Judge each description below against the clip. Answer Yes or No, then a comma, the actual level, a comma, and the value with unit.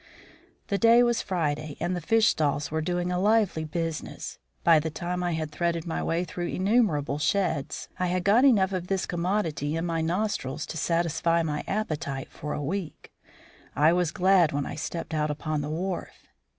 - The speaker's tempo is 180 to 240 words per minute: Yes, average, 185 wpm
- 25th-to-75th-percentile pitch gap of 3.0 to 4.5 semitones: Yes, average, 3.4 semitones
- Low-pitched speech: No, medium, 170 Hz